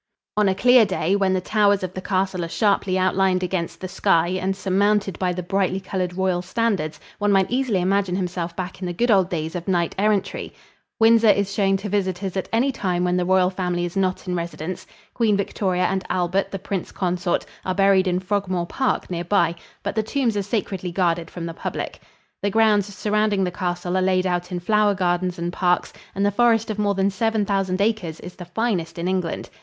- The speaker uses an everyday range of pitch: No, narrow, 2.2 semitones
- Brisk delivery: Yes, fast, 210 wpm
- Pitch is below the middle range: No, high, 190 Hz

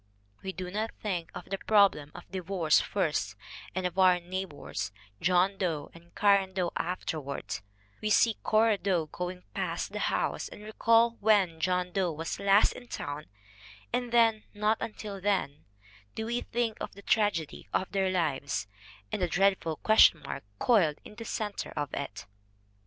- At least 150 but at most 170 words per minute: Yes, average, 165 wpm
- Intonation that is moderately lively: Yes, average, 3.9 semitones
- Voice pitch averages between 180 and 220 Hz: Yes, high, 190 Hz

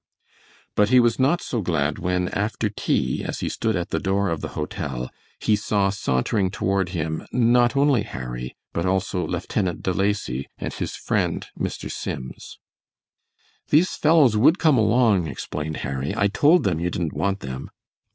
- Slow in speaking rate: No, average, 165 wpm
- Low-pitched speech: Yes, low, 100 Hz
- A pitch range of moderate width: No, wide, 6.0 semitones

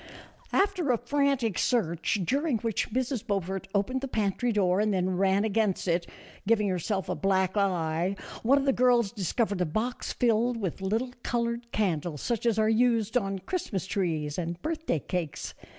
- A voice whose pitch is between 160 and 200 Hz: No, high, 210 Hz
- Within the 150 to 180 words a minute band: Yes, average, 170 wpm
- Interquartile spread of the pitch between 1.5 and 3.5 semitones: No, average, 4.4 semitones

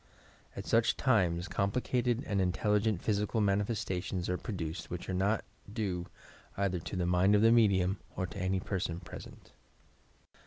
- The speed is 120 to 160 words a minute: Yes, average, 155 wpm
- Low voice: Yes, low, 100 Hz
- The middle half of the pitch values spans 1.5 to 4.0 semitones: Yes, average, 3.1 semitones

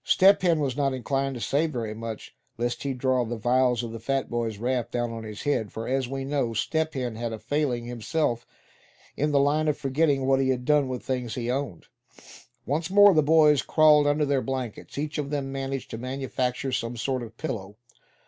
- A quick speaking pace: Yes, fast, 220 wpm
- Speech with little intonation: No, average, 3.4 semitones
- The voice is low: Yes, low, 130 Hz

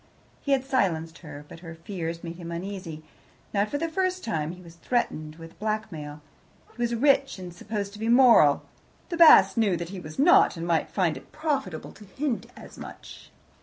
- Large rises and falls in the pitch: Yes, wide, 6.5 semitones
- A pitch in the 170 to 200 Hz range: Yes, high, 190 Hz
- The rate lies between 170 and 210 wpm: Yes, average, 195 wpm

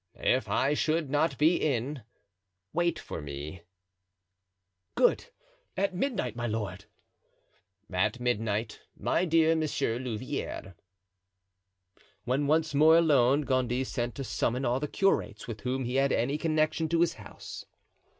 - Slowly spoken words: Yes, slow, 130 wpm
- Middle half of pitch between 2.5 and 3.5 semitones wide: No, average, 4.8 semitones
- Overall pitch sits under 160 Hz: Yes, low, 135 Hz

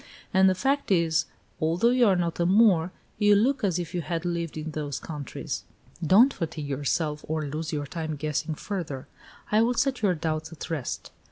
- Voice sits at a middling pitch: Yes, medium, 165 Hz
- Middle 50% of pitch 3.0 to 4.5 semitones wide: Yes, average, 4.1 semitones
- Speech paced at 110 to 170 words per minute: No, average, 190 wpm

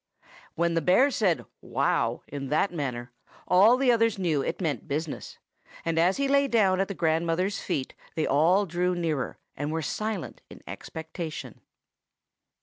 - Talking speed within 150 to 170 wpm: Yes, average, 155 wpm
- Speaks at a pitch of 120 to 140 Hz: No, medium, 170 Hz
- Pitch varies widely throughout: No, average, 4.0 semitones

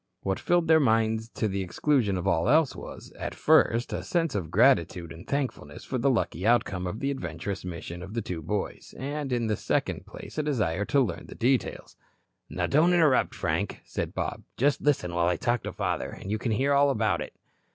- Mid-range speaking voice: No, low, 115 Hz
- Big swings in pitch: Yes, wide, 7.2 semitones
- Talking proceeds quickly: Yes, fast, 210 wpm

